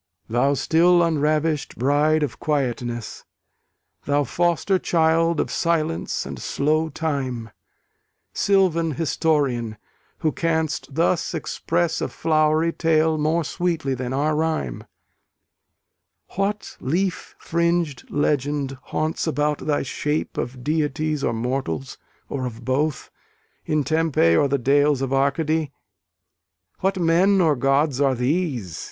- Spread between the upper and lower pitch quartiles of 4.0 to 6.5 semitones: No, average, 3.2 semitones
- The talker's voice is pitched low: No, medium, 150 Hz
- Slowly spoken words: Yes, slow, 115 wpm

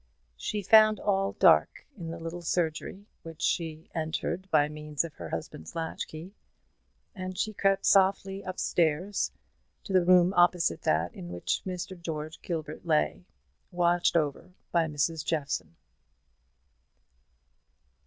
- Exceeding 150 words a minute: No, slow, 135 wpm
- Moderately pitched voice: Yes, medium, 165 Hz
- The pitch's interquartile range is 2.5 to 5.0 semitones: Yes, average, 3.5 semitones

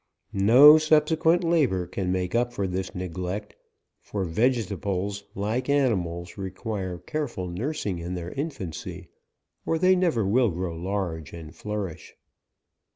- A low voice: Yes, low, 100 Hz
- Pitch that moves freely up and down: Yes, wide, 6.2 semitones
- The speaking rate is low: Yes, slow, 130 wpm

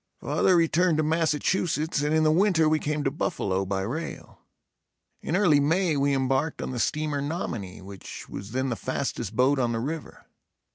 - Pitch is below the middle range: No, medium, 145 Hz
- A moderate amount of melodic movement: Yes, average, 4.0 semitones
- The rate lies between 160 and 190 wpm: Yes, average, 180 wpm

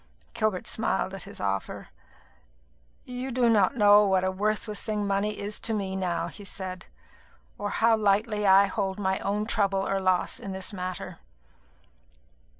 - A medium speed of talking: Yes, average, 155 wpm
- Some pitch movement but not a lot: No, narrow, 1.9 semitones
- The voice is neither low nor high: No, high, 200 Hz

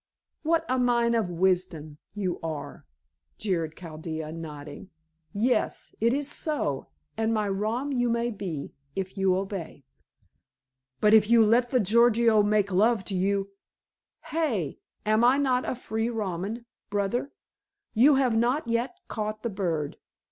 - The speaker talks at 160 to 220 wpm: No, average, 145 wpm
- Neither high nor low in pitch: No, high, 215 Hz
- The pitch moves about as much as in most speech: Yes, average, 4.4 semitones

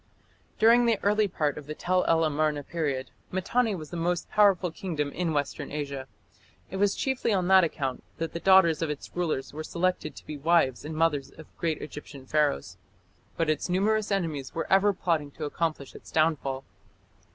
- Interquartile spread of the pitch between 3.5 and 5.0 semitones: Yes, average, 3.9 semitones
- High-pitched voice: No, medium, 165 Hz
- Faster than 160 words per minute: Yes, average, 185 wpm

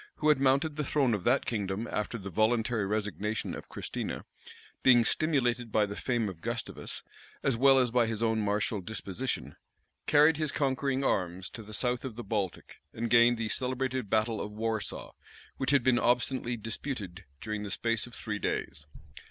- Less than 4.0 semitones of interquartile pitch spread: Yes, average, 3.6 semitones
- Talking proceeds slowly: No, average, 175 wpm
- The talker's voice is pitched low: Yes, low, 115 Hz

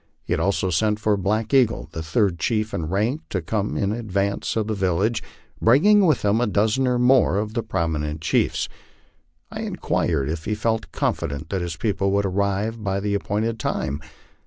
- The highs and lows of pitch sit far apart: No, average, 3.3 semitones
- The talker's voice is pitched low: Yes, low, 105 Hz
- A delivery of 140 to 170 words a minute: No, average, 190 wpm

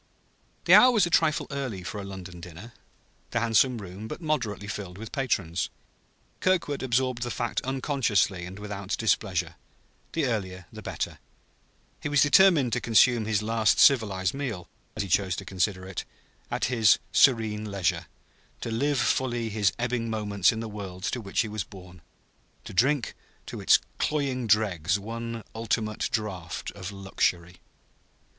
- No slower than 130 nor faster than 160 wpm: Yes, average, 155 wpm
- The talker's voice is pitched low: Yes, low, 110 Hz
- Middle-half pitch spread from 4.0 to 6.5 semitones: Yes, average, 4.5 semitones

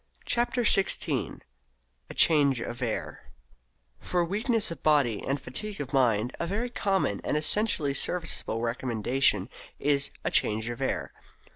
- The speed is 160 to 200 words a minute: No, slow, 135 wpm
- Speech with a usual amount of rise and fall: No, wide, 8.1 semitones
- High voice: No, medium, 140 Hz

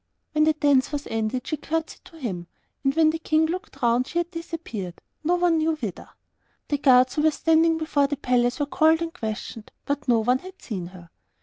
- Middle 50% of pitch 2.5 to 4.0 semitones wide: No, average, 4.8 semitones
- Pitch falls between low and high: No, very high, 290 Hz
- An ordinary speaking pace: No, fast, 210 wpm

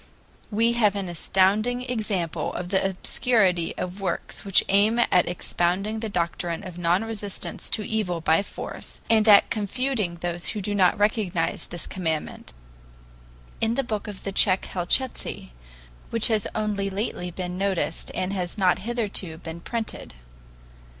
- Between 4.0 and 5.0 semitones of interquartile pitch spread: No, average, 3.6 semitones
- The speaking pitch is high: Yes, high, 195 Hz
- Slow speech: No, average, 150 wpm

